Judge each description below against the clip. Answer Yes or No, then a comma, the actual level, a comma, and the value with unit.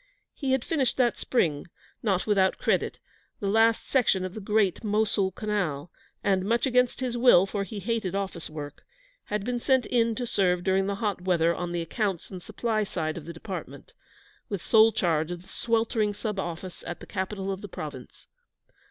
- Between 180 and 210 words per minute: Yes, average, 185 wpm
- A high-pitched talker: Yes, high, 200 Hz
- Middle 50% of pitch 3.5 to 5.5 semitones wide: Yes, average, 4.0 semitones